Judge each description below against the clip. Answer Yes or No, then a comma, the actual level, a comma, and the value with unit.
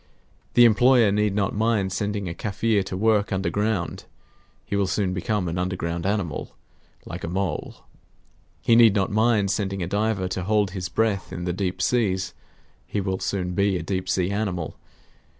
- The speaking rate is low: No, average, 170 wpm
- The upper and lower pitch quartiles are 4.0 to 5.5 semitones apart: No, narrow, 2.4 semitones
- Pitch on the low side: Yes, low, 100 Hz